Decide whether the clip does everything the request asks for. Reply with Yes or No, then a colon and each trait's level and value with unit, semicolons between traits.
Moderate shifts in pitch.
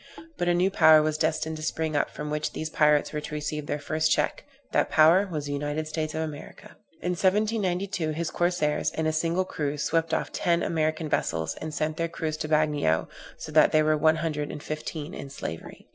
No: narrow, 1.6 semitones